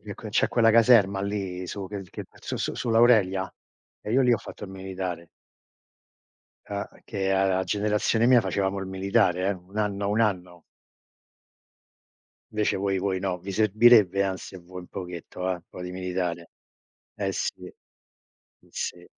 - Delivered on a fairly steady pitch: Yes, narrow, 2.3 semitones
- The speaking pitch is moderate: No, very low, 95 Hz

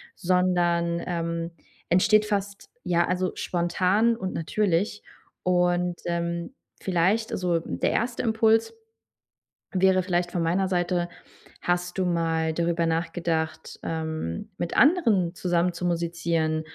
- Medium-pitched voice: Yes, medium, 175 Hz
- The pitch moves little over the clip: Yes, narrow, 1.9 semitones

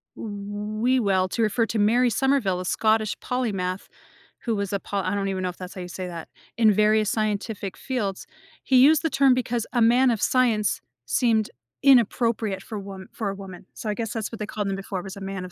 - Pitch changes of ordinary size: Yes, average, 3.3 semitones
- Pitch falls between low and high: No, high, 210 Hz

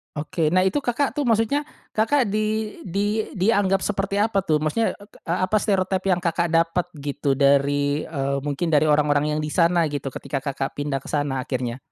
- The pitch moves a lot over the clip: Yes, wide, 5.9 semitones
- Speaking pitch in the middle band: Yes, medium, 170 Hz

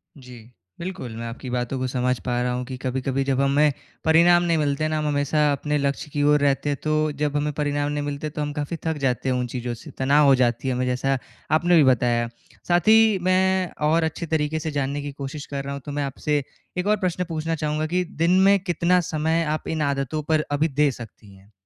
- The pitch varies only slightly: No, average, 3.2 semitones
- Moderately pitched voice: Yes, medium, 145 Hz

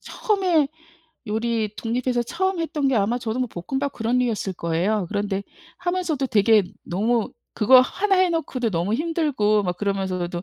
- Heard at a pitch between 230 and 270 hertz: Yes, high, 235 Hz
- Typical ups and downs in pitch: No, wide, 5.8 semitones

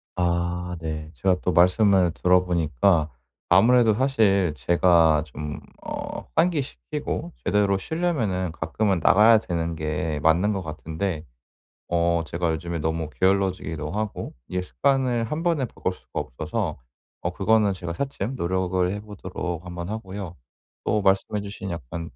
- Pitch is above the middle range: No, very low, 90 Hz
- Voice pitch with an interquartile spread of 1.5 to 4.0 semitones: Yes, average, 3.7 semitones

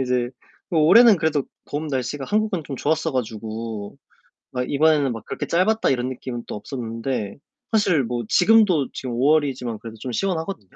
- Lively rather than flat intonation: No, average, 4.9 semitones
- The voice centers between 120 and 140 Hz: Yes, low, 135 Hz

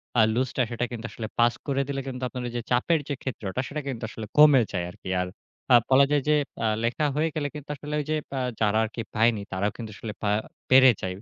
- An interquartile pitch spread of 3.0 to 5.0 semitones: Yes, average, 4.0 semitones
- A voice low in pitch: Yes, low, 125 Hz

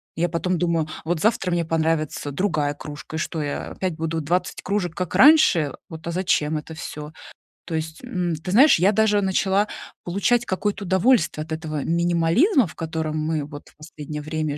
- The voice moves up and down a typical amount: Yes, average, 3.3 semitones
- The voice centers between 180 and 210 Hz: No, medium, 165 Hz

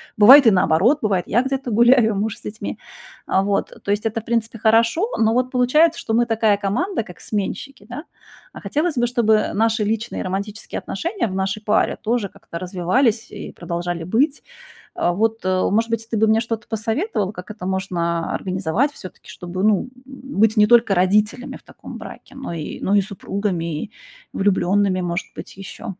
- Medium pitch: No, high, 215 Hz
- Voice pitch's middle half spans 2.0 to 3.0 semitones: No, average, 3.6 semitones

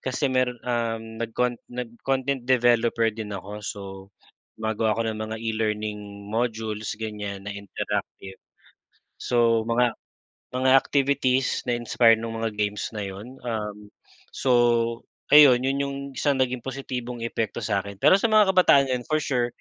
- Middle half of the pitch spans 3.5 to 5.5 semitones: No, average, 2.9 semitones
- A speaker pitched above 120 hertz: No, low, 115 Hz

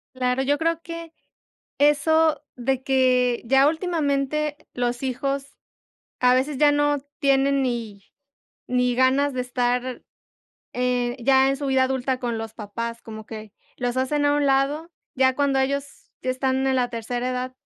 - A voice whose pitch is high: Yes, very high, 265 Hz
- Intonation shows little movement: Yes, narrow, 2.2 semitones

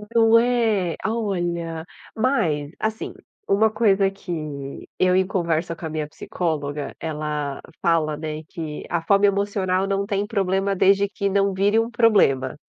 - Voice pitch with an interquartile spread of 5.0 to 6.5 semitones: No, average, 4.3 semitones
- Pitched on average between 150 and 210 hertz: Yes, high, 190 Hz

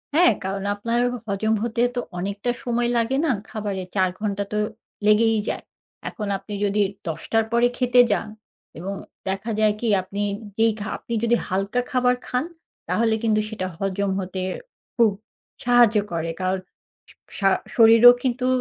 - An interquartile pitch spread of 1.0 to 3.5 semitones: Yes, average, 3.2 semitones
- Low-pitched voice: No, high, 220 Hz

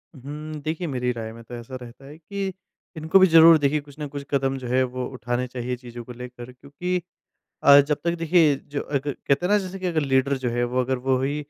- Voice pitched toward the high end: No, medium, 140 Hz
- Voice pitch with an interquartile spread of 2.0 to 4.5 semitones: Yes, average, 3.8 semitones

